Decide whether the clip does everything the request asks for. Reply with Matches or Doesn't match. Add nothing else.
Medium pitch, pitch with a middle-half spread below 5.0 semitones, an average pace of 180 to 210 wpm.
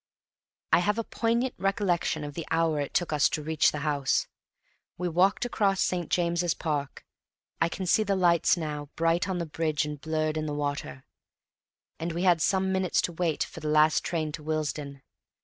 Matches